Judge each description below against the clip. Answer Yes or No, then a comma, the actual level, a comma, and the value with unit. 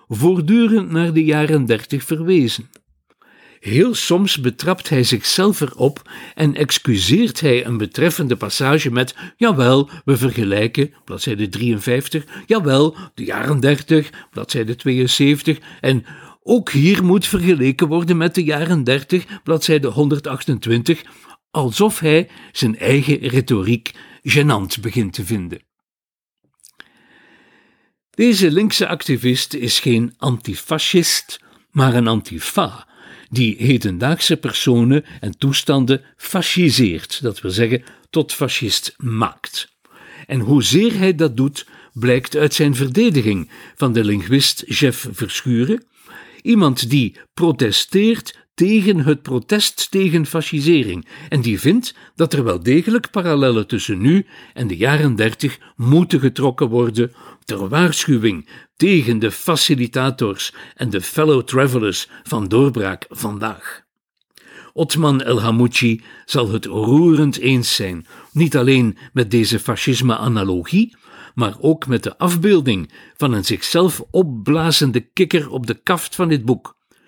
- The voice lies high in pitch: No, medium, 140 Hz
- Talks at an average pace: No, slow, 120 wpm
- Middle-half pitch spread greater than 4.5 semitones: Yes, average, 5.3 semitones